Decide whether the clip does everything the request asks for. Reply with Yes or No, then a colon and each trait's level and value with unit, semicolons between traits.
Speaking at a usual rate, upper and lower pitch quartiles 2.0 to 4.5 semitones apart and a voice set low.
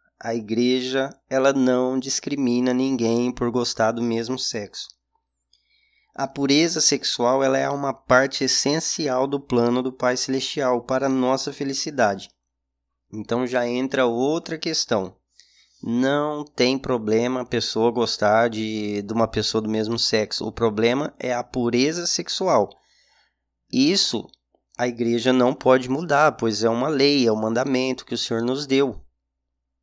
Yes: average, 140 wpm; average, 3.0 semitones; low, 125 Hz